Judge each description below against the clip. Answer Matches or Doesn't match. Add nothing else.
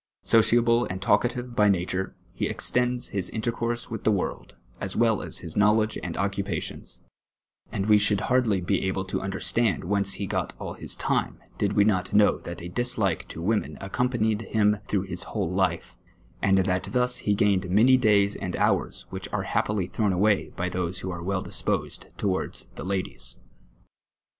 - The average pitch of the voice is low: Matches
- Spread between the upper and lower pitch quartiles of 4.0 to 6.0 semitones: Doesn't match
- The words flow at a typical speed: Matches